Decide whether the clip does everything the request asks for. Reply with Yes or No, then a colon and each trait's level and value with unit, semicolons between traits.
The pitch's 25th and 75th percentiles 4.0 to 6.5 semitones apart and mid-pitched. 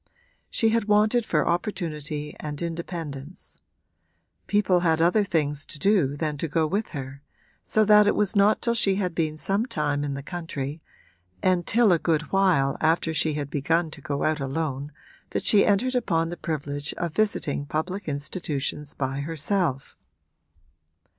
Yes: average, 5.1 semitones; medium, 165 Hz